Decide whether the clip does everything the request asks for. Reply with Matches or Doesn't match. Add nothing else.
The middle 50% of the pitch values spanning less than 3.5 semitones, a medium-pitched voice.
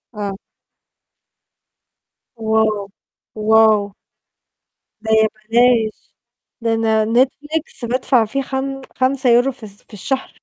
Doesn't match